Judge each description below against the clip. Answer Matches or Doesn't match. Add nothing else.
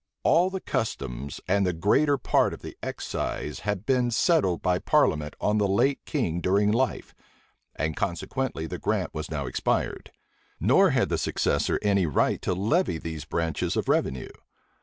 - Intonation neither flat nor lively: Doesn't match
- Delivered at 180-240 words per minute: Doesn't match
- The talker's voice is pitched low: Matches